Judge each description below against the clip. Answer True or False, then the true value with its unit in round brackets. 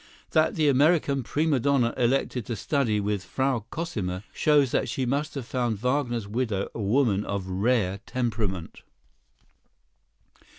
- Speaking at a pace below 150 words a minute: True (135 wpm)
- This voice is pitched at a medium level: False (120 Hz)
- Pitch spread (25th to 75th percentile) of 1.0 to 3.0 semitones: False (5.1 semitones)